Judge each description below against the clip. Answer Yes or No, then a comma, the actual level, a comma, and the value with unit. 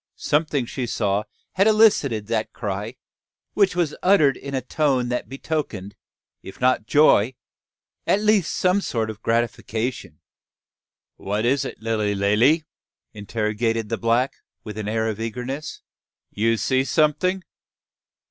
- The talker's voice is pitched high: No, low, 120 Hz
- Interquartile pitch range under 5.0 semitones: No, wide, 5.5 semitones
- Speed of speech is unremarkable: No, slow, 130 wpm